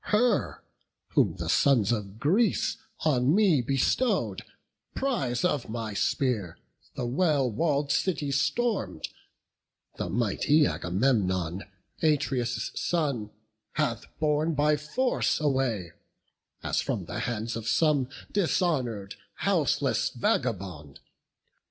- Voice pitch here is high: No, low, 135 Hz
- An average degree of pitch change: No, wide, 6.1 semitones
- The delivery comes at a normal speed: No, slow, 100 wpm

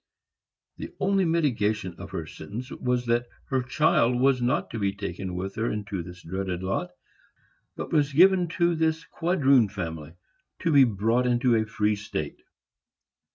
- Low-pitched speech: Yes, low, 120 Hz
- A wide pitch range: Yes, wide, 6.0 semitones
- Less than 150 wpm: No, average, 155 wpm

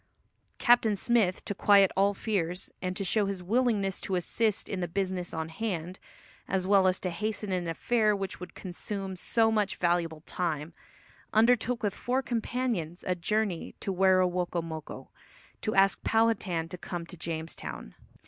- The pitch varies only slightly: No, average, 3.4 semitones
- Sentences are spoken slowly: No, average, 155 wpm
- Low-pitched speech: No, high, 190 Hz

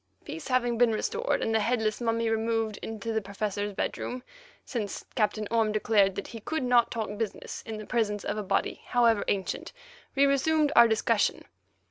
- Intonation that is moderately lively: No, narrow, 2.3 semitones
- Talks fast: No, average, 175 wpm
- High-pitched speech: Yes, high, 225 Hz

